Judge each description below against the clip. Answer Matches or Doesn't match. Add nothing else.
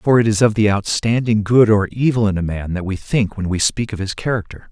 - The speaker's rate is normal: Doesn't match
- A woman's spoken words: Doesn't match